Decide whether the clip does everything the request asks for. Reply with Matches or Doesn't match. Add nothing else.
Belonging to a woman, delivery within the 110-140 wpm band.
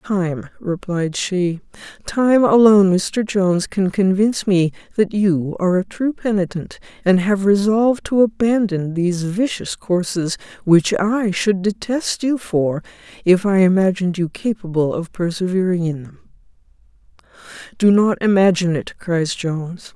Matches